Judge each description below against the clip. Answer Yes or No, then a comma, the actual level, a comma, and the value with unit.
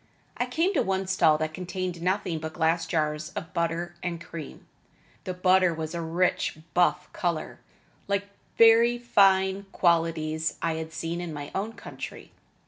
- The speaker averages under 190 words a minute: Yes, average, 155 wpm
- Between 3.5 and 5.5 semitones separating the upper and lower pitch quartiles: No, average, 2.9 semitones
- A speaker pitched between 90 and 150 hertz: No, medium, 175 Hz